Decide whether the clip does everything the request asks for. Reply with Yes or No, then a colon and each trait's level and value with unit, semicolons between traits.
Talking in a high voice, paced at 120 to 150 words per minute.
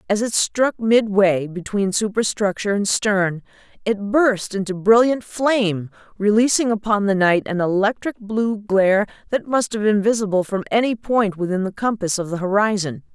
No: high, 205 Hz; average, 160 wpm